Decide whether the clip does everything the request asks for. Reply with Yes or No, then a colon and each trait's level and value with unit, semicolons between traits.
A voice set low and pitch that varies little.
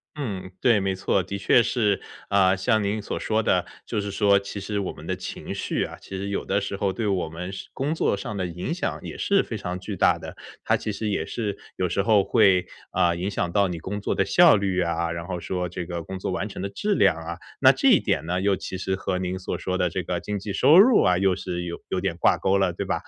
Yes: very low, 95 Hz; narrow, 2.2 semitones